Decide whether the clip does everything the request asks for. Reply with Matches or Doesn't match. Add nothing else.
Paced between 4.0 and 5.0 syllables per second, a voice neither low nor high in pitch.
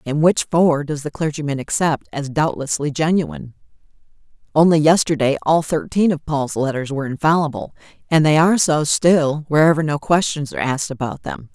Doesn't match